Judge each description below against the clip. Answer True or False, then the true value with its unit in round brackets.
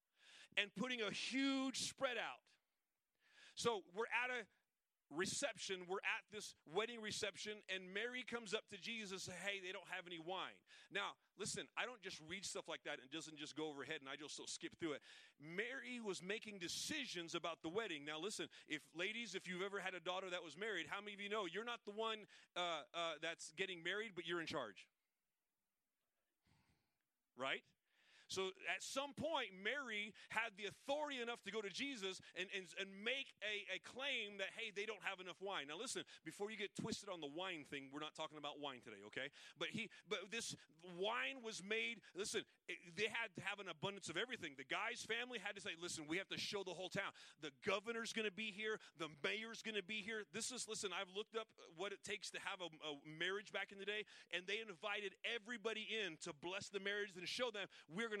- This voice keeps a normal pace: False (220 wpm)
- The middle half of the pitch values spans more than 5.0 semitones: False (3.9 semitones)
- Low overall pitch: False (200 Hz)